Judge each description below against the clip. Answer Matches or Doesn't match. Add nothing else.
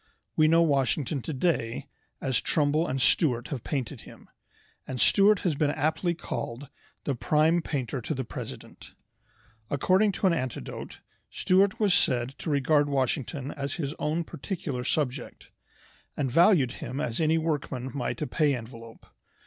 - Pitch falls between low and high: Matches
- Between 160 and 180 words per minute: Doesn't match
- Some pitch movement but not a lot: Matches